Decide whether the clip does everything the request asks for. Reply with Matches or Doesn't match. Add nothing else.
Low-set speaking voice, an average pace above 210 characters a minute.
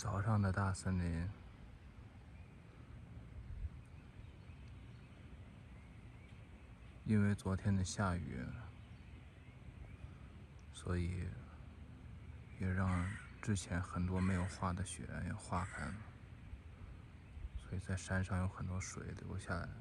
Doesn't match